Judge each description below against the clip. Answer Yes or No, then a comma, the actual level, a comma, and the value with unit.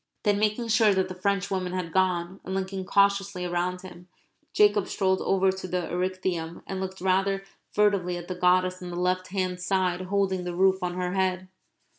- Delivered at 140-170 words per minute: No, average, 185 wpm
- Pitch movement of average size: No, narrow, 1.2 semitones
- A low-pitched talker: No, medium, 185 Hz